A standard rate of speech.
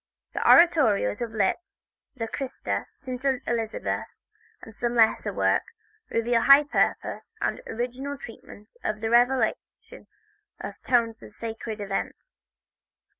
No: slow, 120 wpm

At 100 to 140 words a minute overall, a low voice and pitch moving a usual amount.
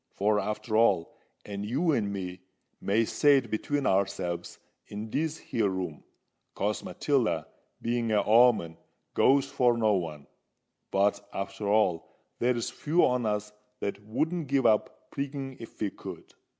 Yes: slow, 135 wpm; low, 110 Hz; average, 4.1 semitones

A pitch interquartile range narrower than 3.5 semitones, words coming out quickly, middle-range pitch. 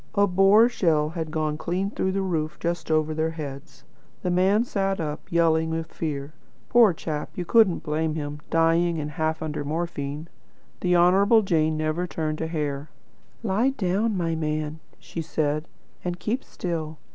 No: average, 2.9 semitones; average, 165 wpm; medium, 165 Hz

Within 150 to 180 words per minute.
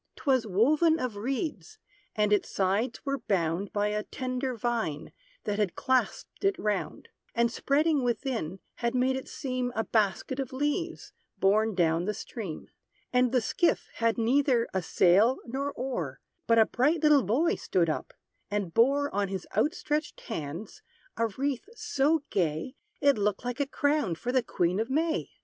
Yes: average, 165 wpm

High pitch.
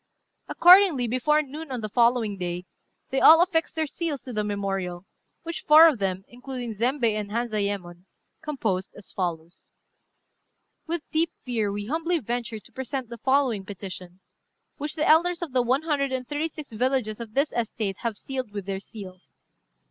Yes: high, 240 Hz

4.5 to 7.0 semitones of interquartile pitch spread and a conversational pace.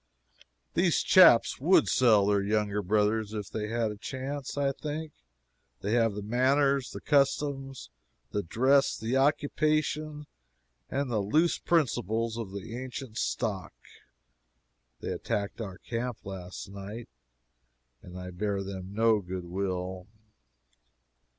No: average, 5.2 semitones; slow, 125 wpm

